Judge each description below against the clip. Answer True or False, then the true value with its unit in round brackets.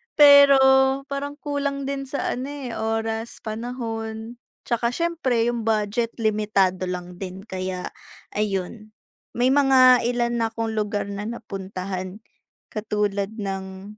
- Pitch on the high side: True (225 Hz)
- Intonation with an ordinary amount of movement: True (3.8 semitones)